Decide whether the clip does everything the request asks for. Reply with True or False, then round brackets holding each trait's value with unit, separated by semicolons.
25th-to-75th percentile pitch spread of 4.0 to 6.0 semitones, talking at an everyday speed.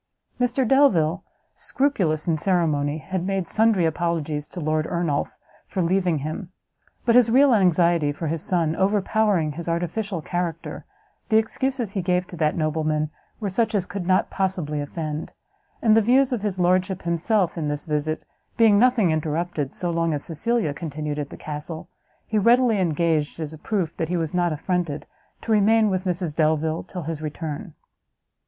True (4.4 semitones; 170 wpm)